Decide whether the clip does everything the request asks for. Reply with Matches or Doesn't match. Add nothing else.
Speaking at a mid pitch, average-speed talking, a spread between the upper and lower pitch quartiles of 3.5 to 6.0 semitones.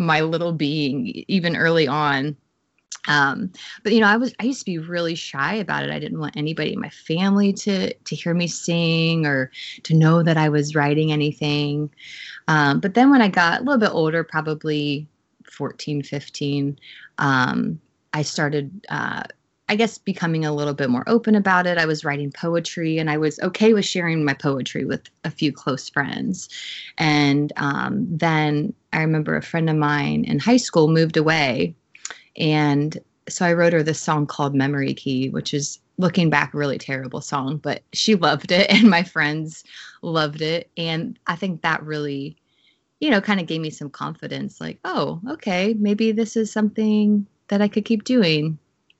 Matches